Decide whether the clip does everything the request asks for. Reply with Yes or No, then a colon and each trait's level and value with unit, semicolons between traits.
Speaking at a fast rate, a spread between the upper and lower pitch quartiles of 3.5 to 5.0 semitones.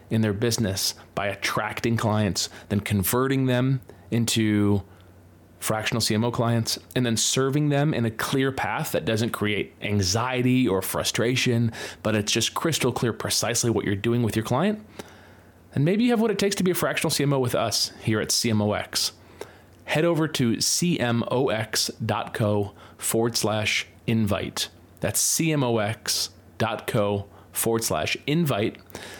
No: average, 140 wpm; average, 3.8 semitones